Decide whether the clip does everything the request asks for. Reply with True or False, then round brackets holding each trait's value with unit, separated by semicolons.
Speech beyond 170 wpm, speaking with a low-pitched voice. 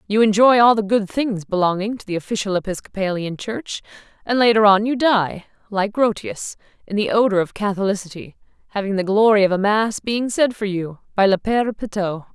False (185 wpm; 205 Hz)